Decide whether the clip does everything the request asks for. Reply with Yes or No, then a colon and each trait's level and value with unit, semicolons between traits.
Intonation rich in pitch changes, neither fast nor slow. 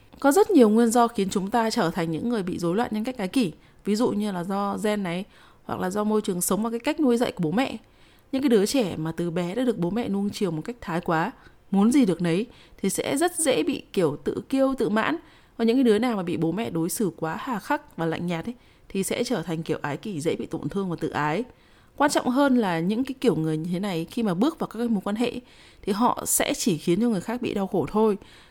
No: wide, 5.7 semitones; fast, 285 wpm